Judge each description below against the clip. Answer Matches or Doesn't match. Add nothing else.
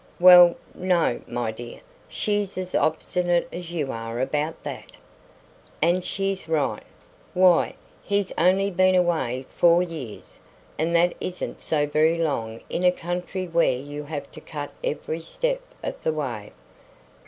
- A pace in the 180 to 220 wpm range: Doesn't match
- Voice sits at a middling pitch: Matches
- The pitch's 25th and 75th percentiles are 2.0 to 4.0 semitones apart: Matches